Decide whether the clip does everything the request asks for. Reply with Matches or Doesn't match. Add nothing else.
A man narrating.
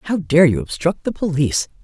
Doesn't match